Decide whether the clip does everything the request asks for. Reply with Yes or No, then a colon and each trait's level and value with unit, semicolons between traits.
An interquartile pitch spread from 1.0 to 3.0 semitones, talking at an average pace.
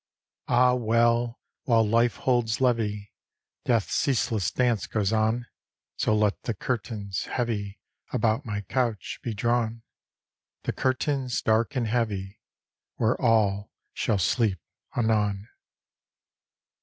No: narrow, 2.5 semitones; slow, 110 wpm